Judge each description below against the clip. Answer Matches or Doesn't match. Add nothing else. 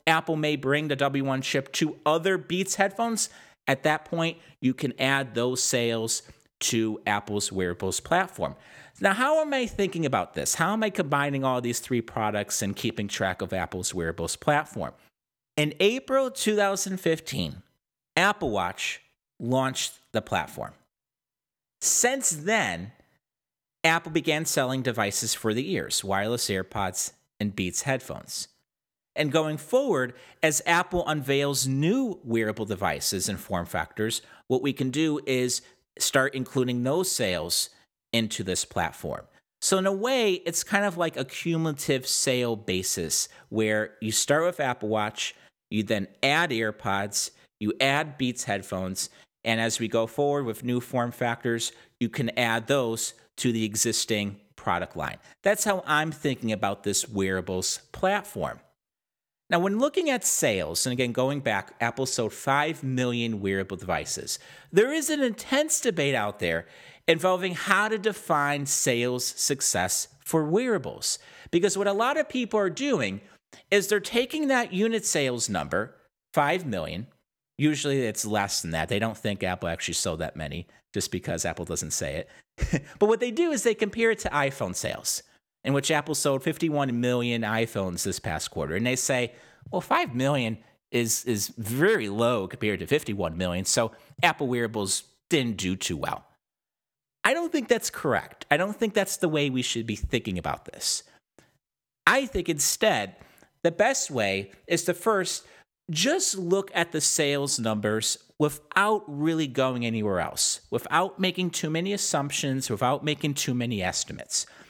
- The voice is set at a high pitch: Doesn't match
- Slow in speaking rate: Doesn't match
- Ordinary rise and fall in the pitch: Doesn't match